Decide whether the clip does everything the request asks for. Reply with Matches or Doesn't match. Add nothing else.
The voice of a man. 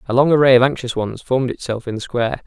Matches